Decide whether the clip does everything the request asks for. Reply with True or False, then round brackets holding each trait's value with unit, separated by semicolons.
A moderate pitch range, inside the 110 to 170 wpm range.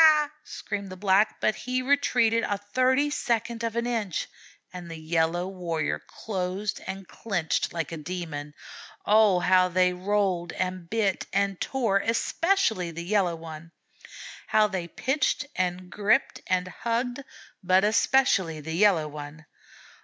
True (4.3 semitones; 140 wpm)